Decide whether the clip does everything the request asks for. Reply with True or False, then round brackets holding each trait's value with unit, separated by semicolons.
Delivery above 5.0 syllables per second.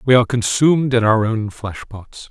True (5.2 syllables/s)